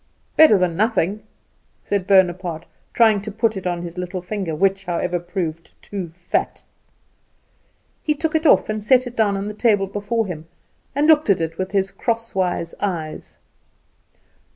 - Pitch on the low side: No, high, 195 Hz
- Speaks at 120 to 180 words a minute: Yes, average, 160 wpm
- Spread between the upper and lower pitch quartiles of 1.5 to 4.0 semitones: Yes, average, 3.5 semitones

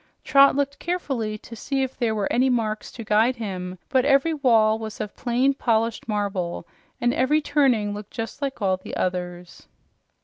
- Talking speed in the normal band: Yes, average, 175 wpm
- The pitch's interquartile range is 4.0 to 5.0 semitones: Yes, average, 4.3 semitones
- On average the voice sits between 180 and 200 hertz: No, high, 230 Hz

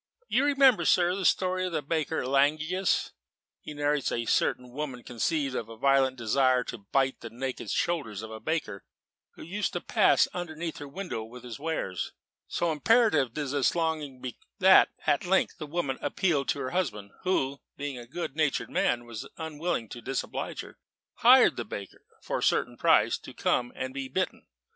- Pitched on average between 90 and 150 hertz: Yes, medium, 140 Hz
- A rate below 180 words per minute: No, average, 185 wpm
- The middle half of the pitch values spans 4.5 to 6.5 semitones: Yes, average, 5.2 semitones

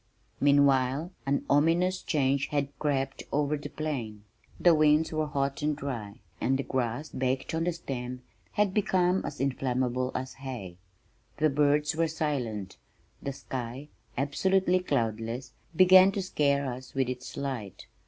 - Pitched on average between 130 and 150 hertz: Yes, medium, 140 Hz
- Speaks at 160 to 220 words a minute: No, average, 145 wpm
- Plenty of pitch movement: No, average, 3.3 semitones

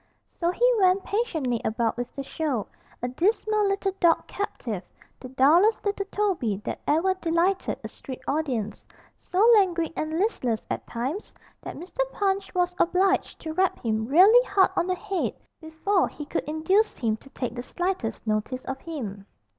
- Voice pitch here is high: Yes, very high, 335 Hz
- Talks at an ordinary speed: Yes, average, 165 wpm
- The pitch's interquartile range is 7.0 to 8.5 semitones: Yes, wide, 7.3 semitones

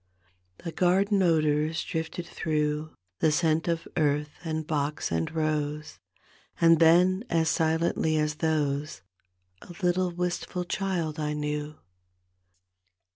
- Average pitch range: No, narrow, 2.3 semitones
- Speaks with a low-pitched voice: No, medium, 160 Hz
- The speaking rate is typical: No, slow, 115 wpm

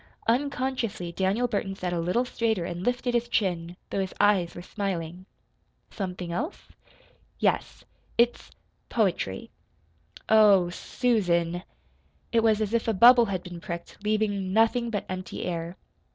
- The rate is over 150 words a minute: No, slow, 135 wpm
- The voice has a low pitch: No, high, 200 Hz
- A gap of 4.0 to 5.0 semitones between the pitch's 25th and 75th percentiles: Yes, average, 4.6 semitones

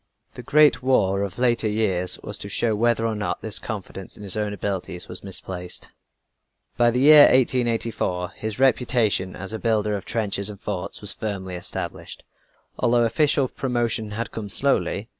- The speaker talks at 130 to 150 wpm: No, average, 165 wpm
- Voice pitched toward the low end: Yes, low, 110 Hz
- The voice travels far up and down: No, average, 3.3 semitones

